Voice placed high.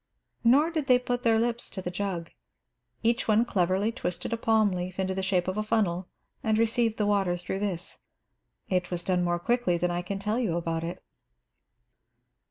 Yes: high, 195 Hz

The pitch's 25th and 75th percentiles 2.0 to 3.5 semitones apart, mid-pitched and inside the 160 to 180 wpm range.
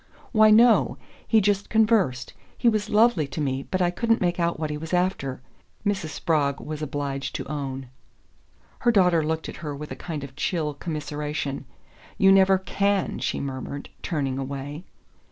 No: average, 5.3 semitones; medium, 160 Hz; average, 170 wpm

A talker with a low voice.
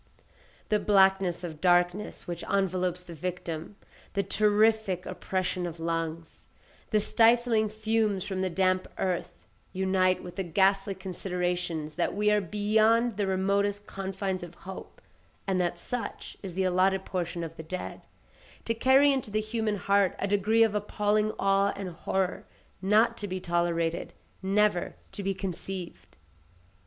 No: high, 190 Hz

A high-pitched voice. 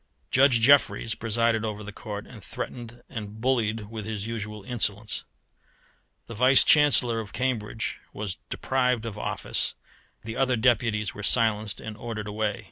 No: low, 110 Hz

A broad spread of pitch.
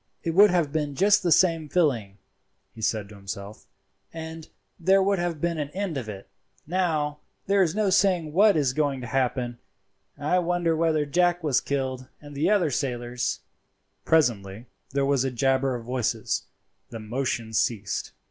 Yes: wide, 5.8 semitones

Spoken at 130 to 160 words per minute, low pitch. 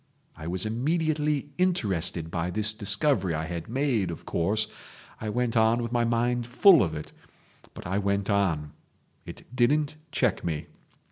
Yes: average, 145 wpm; low, 110 Hz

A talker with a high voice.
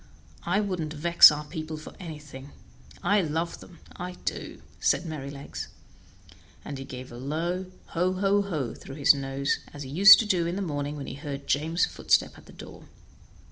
No: medium, 155 Hz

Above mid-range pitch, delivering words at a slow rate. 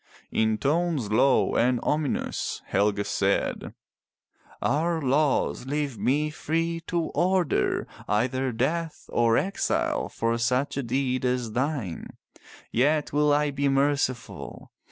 No: low, 135 Hz; slow, 115 wpm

